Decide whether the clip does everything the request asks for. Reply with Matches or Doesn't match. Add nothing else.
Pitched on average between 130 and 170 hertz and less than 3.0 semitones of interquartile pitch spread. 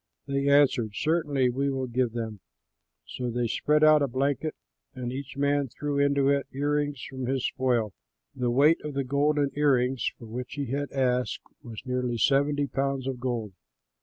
Matches